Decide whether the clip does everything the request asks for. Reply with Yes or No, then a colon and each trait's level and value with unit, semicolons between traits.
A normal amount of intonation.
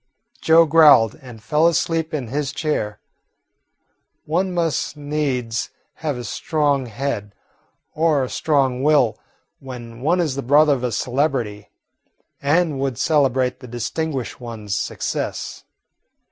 Yes: average, 4.0 semitones